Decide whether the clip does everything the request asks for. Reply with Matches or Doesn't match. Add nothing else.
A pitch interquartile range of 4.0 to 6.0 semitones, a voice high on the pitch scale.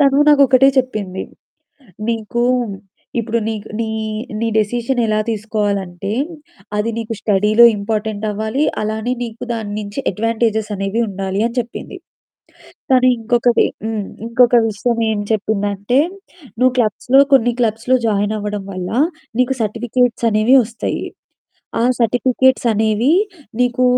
Doesn't match